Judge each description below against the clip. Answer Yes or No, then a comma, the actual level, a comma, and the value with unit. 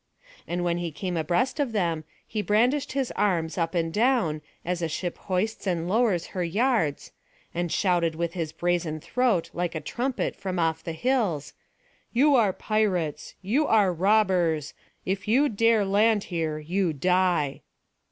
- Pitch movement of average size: Yes, average, 4.6 semitones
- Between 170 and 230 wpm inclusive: No, average, 160 wpm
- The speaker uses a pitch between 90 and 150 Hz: No, medium, 180 Hz